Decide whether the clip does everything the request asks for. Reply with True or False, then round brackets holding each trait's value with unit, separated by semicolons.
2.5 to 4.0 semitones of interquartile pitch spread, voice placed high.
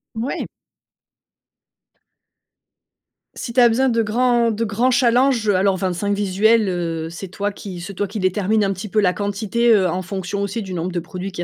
True (3.5 semitones; 200 Hz)